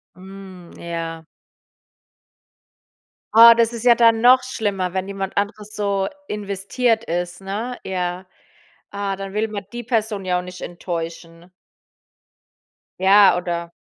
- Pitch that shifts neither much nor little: Yes, average, 3.5 semitones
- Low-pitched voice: No, high, 195 Hz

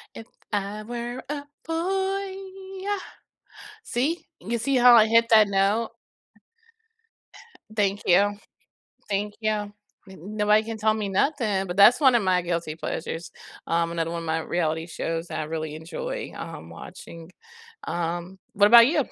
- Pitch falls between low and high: No, high, 205 Hz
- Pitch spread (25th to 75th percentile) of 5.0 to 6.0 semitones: Yes, wide, 5.6 semitones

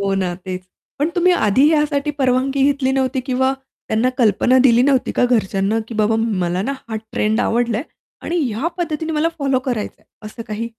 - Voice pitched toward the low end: No, very high, 250 Hz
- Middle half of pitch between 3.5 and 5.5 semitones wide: Yes, average, 4.3 semitones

